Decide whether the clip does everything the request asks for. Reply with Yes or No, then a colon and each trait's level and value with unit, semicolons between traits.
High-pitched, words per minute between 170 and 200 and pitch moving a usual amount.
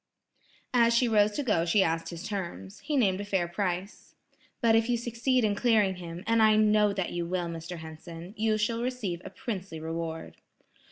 Yes: high, 200 Hz; average, 190 wpm; average, 4.8 semitones